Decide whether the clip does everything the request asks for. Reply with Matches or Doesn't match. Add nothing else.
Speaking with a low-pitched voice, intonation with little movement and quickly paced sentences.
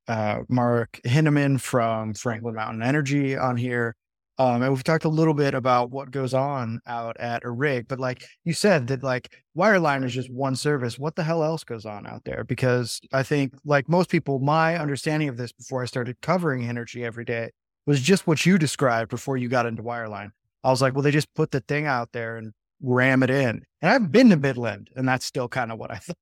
Doesn't match